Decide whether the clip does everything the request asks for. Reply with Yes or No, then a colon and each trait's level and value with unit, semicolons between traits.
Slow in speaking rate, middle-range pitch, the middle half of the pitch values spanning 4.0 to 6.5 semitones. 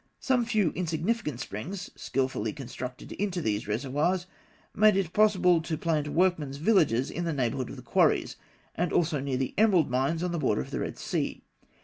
No: average, 175 wpm; medium, 160 Hz; wide, 5.6 semitones